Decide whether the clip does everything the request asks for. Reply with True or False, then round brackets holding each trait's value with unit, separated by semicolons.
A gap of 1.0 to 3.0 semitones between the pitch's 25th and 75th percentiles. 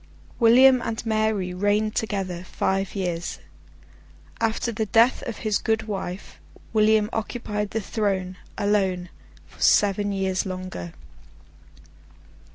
True (2.7 semitones)